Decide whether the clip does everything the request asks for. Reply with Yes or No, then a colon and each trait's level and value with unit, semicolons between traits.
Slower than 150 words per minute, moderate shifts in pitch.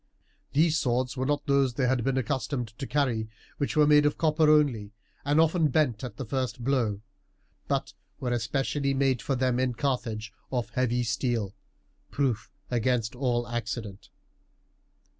No: average, 155 wpm; average, 3.1 semitones